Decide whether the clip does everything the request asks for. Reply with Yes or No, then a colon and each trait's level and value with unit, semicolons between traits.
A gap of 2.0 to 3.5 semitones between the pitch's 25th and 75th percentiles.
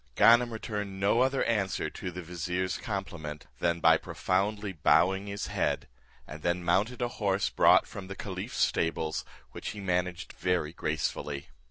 Yes: average, 3.2 semitones